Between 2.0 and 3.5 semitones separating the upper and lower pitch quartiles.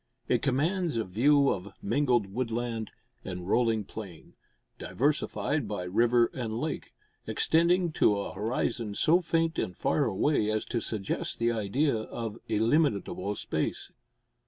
No: wide, 5.6 semitones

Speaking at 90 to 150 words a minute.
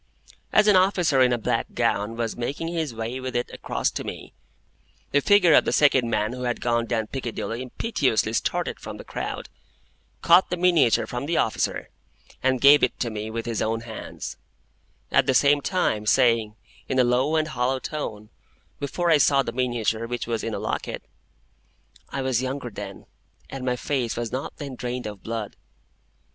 No: average, 180 wpm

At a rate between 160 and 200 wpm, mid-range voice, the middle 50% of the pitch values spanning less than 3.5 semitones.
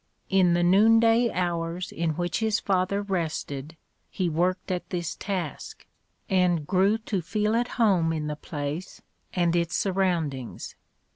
No: average, 145 wpm; medium, 180 Hz; average, 3.0 semitones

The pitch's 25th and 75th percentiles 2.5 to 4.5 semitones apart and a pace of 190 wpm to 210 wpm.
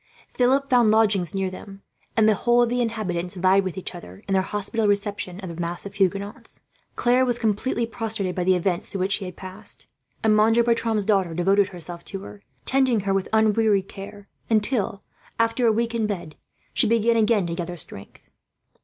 Yes: average, 3.2 semitones; average, 195 wpm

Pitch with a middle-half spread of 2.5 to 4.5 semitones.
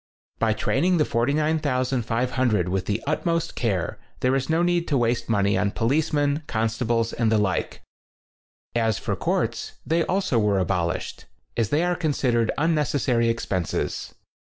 No: wide, 5.4 semitones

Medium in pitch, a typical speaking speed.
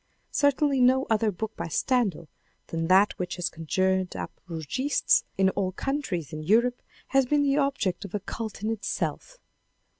No: high, 210 Hz; average, 160 wpm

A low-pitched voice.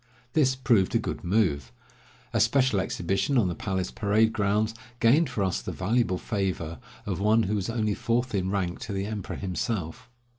Yes: low, 105 Hz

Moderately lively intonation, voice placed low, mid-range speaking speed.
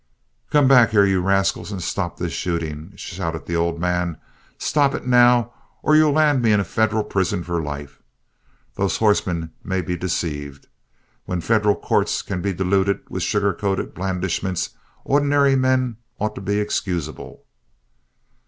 Yes: average, 4.4 semitones; very low, 95 Hz; average, 155 wpm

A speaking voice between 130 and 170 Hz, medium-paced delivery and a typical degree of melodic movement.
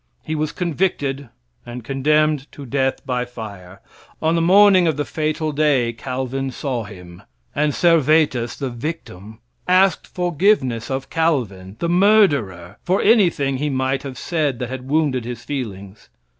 Yes: low, 135 Hz; average, 145 wpm; average, 4.8 semitones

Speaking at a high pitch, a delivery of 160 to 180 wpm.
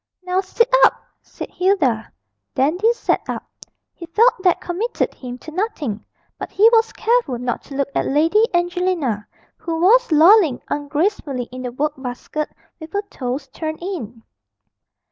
No: very high, 325 Hz; average, 150 wpm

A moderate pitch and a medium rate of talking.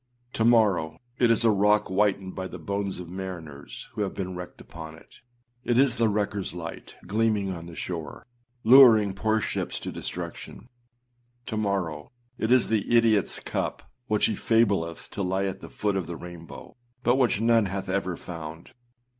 No: low, 100 Hz; average, 180 wpm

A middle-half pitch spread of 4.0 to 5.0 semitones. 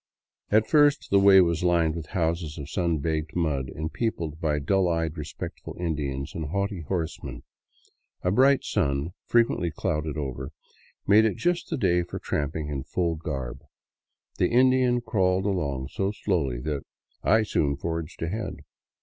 Yes: average, 4.6 semitones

